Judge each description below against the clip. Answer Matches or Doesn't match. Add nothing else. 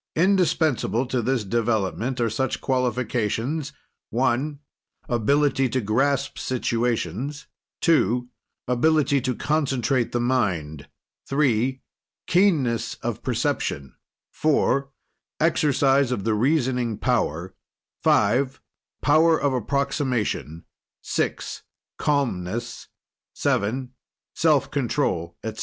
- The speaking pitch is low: Matches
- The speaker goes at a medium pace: Doesn't match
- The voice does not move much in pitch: Doesn't match